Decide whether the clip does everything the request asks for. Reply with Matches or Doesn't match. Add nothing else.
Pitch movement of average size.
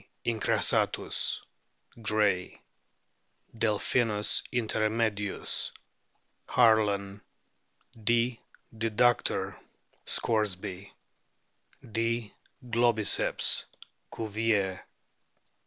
Doesn't match